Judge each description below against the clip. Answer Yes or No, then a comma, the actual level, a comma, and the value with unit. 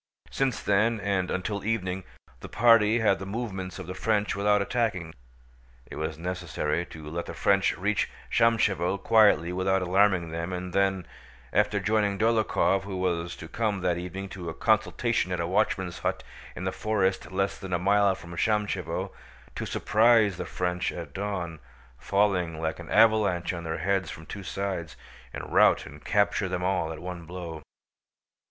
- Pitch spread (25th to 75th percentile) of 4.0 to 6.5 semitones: No, average, 2.9 semitones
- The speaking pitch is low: Yes, very low, 95 Hz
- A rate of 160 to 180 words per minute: Yes, average, 170 wpm